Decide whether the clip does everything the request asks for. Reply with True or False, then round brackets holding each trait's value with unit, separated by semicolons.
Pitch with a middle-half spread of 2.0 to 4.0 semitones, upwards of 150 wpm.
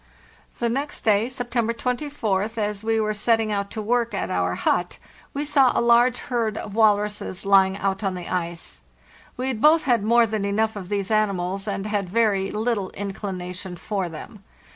True (3.1 semitones; 180 wpm)